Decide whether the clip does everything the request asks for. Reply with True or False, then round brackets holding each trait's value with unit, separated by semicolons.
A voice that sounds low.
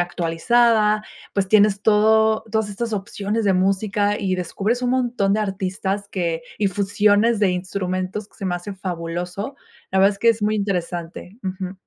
False (200 Hz)